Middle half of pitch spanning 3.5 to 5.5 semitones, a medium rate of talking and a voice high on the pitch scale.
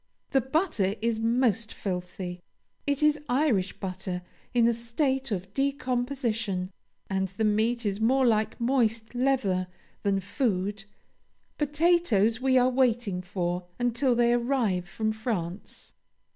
No: average, 4.9 semitones; slow, 125 wpm; high, 230 Hz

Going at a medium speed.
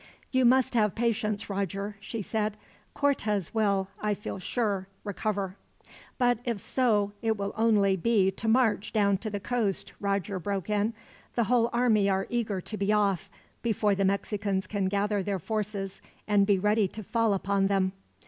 Yes: average, 165 wpm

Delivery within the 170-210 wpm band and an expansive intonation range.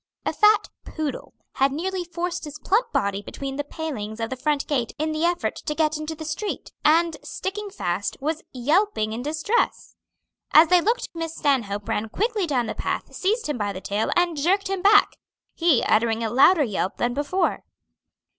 Yes: average, 185 wpm; wide, 6.3 semitones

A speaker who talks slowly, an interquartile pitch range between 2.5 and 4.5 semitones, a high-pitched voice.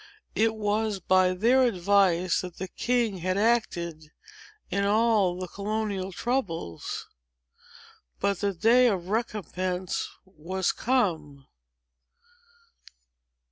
Yes: slow, 100 wpm; average, 3.5 semitones; high, 195 Hz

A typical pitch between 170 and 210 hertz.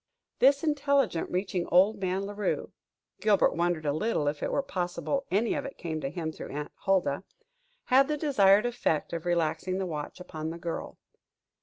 Yes: medium, 185 Hz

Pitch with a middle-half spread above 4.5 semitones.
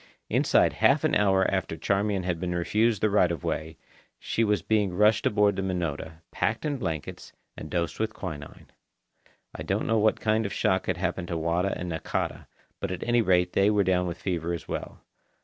No: average, 3.3 semitones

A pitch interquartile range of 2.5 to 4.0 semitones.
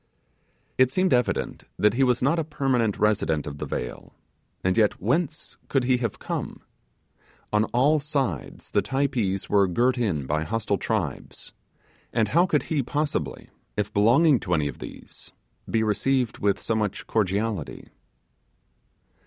No: average, 5.1 semitones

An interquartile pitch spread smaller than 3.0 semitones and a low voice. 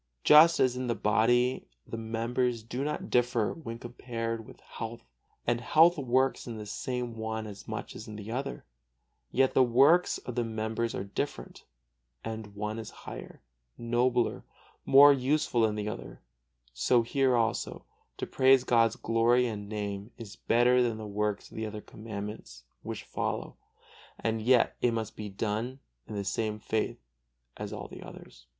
Yes: narrow, 2.5 semitones; low, 115 Hz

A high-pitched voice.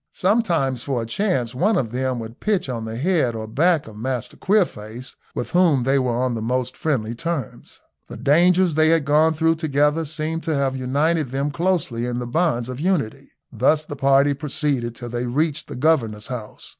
No: medium, 140 Hz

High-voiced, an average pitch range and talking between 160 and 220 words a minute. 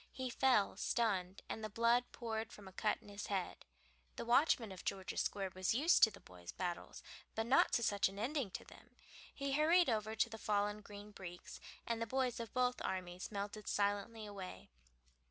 Yes: high, 215 Hz; average, 3.2 semitones; average, 190 wpm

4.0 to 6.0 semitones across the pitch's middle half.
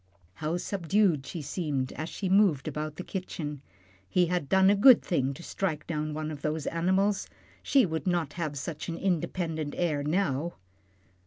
No: average, 3.6 semitones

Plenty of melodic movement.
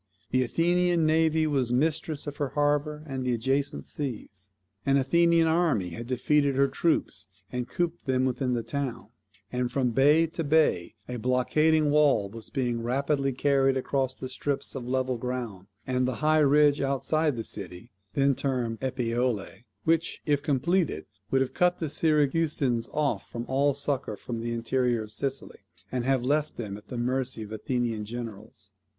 No: average, 3.7 semitones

